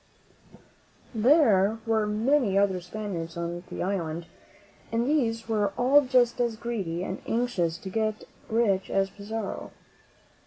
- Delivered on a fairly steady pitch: No, average, 3.7 semitones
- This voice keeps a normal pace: No, slow, 125 wpm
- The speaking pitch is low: No, high, 215 Hz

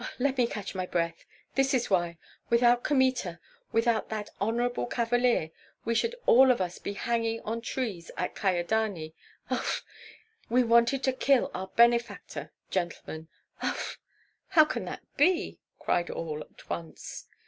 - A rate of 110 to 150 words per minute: Yes, average, 140 wpm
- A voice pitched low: No, high, 230 Hz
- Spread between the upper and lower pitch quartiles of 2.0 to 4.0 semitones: No, average, 5.2 semitones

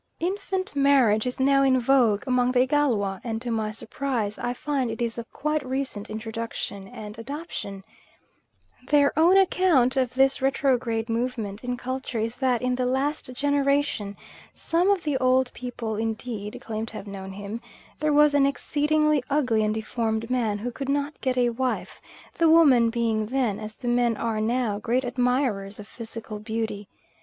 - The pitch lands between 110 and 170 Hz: No, high, 245 Hz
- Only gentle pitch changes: No, average, 3.8 semitones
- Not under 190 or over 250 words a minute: No, average, 170 wpm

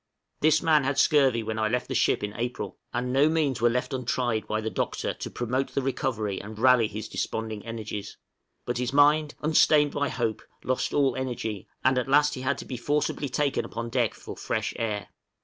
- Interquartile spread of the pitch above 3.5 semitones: Yes, average, 3.9 semitones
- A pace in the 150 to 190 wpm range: No, average, 200 wpm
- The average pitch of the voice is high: No, low, 125 Hz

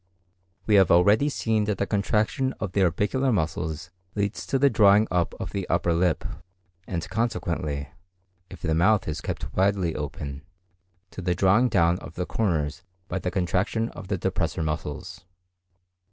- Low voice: Yes, very low, 95 Hz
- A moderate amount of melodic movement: Yes, average, 3.8 semitones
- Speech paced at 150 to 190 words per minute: Yes, average, 160 wpm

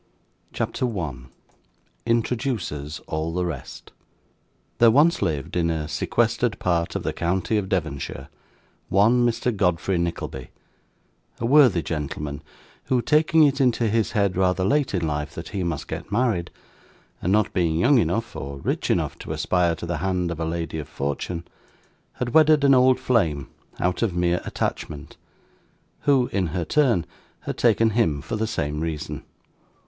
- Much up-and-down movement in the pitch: Yes, wide, 6.2 semitones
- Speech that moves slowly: No, average, 155 wpm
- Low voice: Yes, very low, 90 Hz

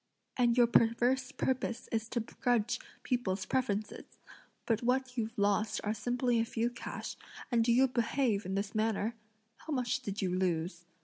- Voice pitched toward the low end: No, high, 230 Hz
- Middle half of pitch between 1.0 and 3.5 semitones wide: Yes, average, 3.1 semitones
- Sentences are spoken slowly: No, average, 165 wpm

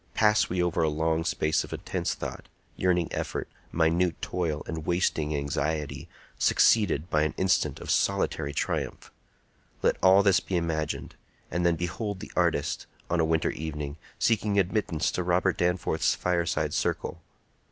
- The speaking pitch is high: No, very low, 85 Hz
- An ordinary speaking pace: Yes, average, 150 wpm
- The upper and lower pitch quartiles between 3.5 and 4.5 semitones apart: No, average, 2.7 semitones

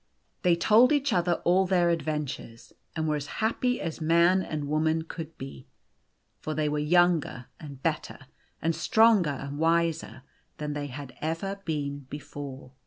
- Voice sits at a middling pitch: Yes, medium, 160 Hz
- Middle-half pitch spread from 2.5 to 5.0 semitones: Yes, average, 3.2 semitones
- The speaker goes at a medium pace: Yes, average, 155 wpm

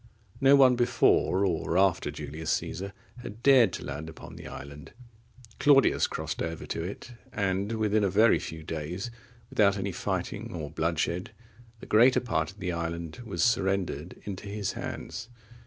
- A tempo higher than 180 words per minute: No, average, 155 wpm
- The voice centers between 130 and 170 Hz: No, very low, 95 Hz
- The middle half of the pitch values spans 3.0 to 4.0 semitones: No, average, 4.8 semitones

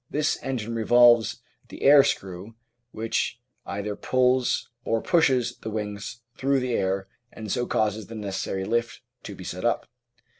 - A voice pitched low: Yes, low, 115 Hz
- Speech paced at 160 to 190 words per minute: No, average, 150 wpm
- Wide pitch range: No, average, 3.5 semitones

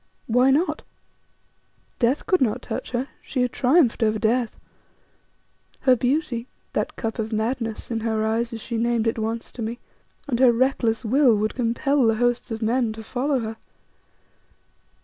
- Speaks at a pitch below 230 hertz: No, high, 235 Hz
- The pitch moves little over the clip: Yes, narrow, 2.3 semitones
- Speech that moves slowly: No, average, 165 wpm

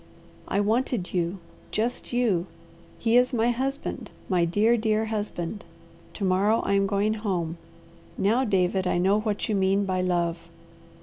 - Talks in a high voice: Yes, high, 200 Hz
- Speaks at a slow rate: No, average, 150 wpm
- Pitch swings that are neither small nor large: Yes, average, 3.3 semitones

